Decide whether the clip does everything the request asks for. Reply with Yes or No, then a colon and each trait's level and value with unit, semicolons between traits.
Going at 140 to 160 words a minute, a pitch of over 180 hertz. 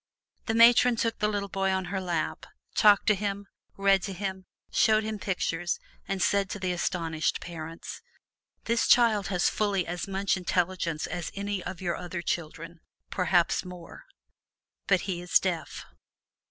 Yes: average, 155 wpm; high, 190 Hz